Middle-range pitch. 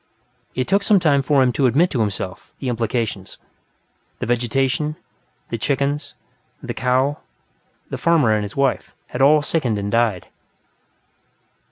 No: low, 130 Hz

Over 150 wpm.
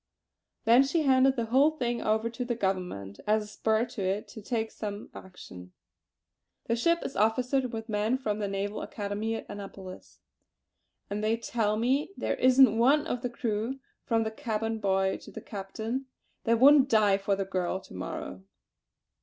Yes: average, 175 wpm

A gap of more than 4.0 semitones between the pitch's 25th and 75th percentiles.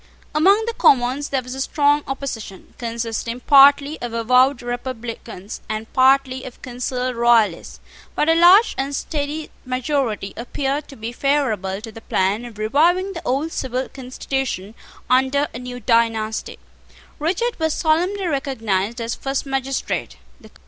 No: average, 3.7 semitones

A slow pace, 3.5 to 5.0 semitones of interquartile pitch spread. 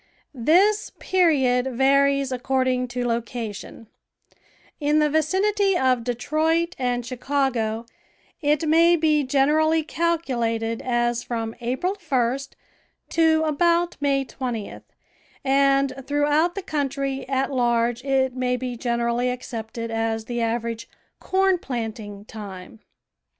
Yes: slow, 115 wpm; average, 4.4 semitones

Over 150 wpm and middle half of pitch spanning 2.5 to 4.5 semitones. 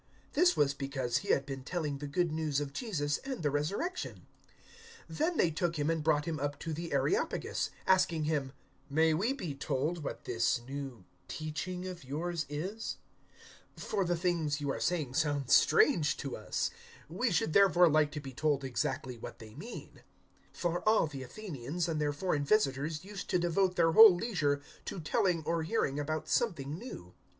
Yes: average, 185 wpm; average, 3.9 semitones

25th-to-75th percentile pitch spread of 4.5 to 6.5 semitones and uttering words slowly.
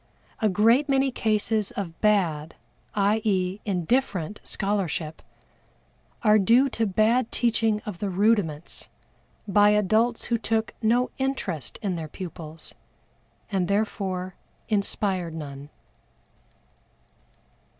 No: average, 3.6 semitones; slow, 105 wpm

